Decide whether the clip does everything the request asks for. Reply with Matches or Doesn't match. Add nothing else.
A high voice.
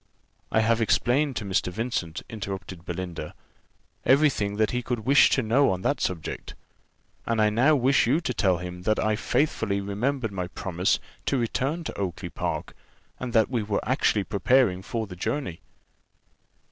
Doesn't match